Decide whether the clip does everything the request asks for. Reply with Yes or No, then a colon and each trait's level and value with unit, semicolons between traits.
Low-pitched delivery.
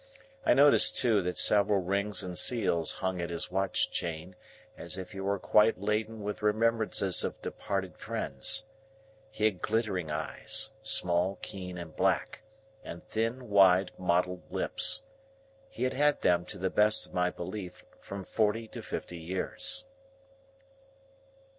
Yes: low, 100 Hz